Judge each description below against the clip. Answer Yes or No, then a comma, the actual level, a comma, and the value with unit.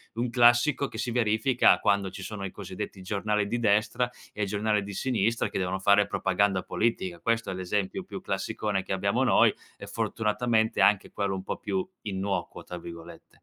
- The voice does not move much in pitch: No, average, 3.1 semitones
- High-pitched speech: No, low, 105 Hz